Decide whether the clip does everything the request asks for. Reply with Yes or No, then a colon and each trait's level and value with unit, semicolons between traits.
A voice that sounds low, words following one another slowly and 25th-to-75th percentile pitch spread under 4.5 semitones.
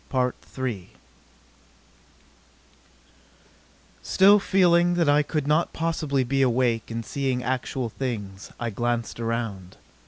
No: low, 130 Hz; slow, 95 wpm; average, 4.9 semitones